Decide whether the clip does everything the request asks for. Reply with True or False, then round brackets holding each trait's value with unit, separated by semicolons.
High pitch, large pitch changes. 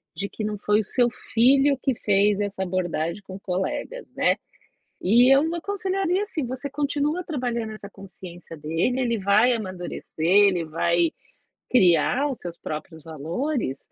True (210 Hz; 7.0 semitones)